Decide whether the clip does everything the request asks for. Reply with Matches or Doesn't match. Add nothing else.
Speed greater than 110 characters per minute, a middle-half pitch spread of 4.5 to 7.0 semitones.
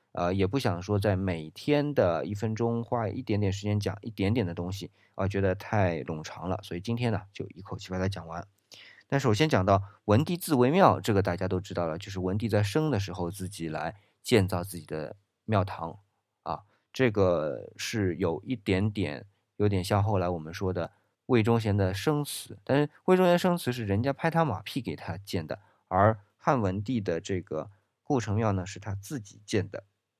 Doesn't match